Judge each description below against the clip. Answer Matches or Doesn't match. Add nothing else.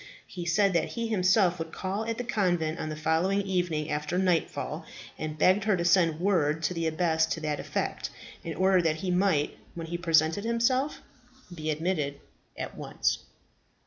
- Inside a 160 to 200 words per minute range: Matches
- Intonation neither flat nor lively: Matches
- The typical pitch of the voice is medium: Matches